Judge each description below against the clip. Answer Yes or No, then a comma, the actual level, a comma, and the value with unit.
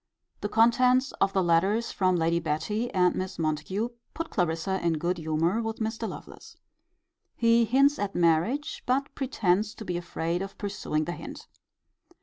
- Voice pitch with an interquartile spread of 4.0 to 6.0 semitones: Yes, average, 5.2 semitones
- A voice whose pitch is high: Yes, high, 195 Hz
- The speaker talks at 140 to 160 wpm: Yes, average, 155 wpm